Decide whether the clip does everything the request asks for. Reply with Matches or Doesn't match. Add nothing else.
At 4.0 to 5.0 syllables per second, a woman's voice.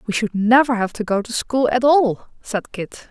Matches